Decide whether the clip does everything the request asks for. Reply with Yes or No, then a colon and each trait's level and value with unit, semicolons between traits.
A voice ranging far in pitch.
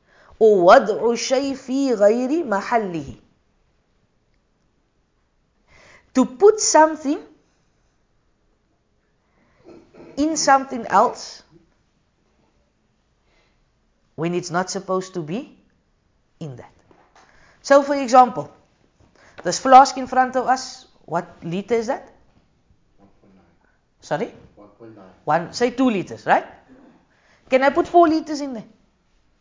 Yes: wide, 7.9 semitones